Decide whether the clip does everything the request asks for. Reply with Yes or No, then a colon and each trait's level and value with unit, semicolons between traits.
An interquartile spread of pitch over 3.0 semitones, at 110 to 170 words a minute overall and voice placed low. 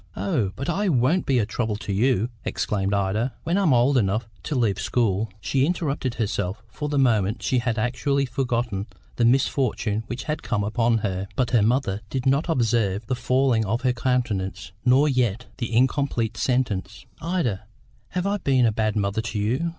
No: average, 3.9 semitones; average, 185 wpm; low, 120 Hz